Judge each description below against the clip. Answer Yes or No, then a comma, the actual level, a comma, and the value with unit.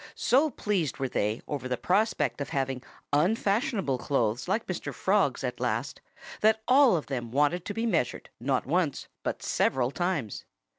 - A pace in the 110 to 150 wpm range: No, average, 160 wpm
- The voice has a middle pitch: Yes, medium, 150 Hz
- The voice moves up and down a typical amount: No, wide, 8.0 semitones